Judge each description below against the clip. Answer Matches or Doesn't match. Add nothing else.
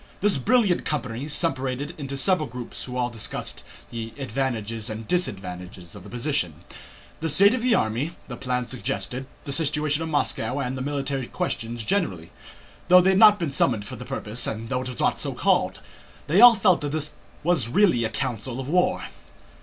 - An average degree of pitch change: Doesn't match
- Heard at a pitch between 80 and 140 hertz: Matches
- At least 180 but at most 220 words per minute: Matches